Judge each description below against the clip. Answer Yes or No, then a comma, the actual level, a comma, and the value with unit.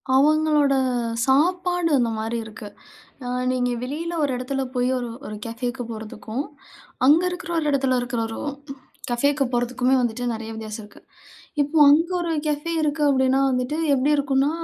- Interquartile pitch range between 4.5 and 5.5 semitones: No, average, 3.6 semitones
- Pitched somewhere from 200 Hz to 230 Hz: No, very high, 265 Hz